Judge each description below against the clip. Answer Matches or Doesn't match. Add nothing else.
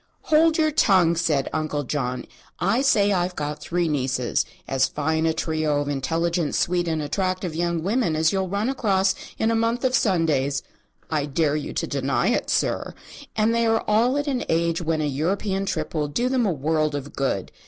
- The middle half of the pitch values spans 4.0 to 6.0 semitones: Matches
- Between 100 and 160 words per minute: Doesn't match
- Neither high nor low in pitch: Matches